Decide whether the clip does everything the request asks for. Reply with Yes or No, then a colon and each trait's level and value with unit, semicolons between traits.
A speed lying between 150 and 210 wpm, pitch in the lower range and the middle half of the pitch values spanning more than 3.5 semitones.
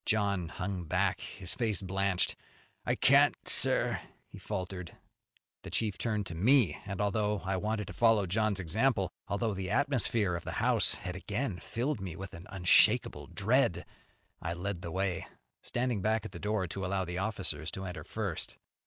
No: average, 170 wpm; low, 100 Hz; average, 3.0 semitones